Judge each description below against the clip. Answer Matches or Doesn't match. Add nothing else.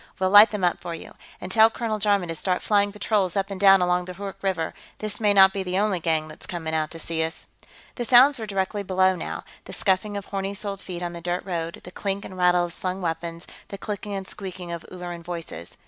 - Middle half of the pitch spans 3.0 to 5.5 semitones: Doesn't match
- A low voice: Doesn't match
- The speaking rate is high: Matches